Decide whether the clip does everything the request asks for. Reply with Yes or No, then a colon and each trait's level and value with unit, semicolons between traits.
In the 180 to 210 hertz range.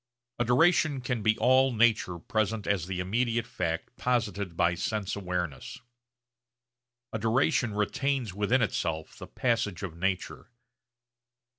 No: low, 110 Hz